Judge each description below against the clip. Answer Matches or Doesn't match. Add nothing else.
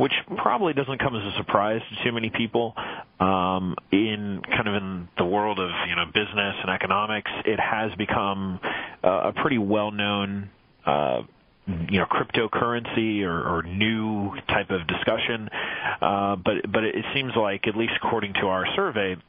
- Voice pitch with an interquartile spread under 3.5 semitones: Matches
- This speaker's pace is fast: Doesn't match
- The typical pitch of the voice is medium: Doesn't match